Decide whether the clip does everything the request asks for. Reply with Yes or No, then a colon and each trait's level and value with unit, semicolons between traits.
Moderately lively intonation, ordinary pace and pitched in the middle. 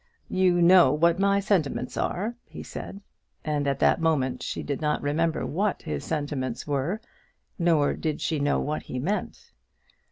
Yes: average, 4.0 semitones; average, 155 wpm; medium, 155 Hz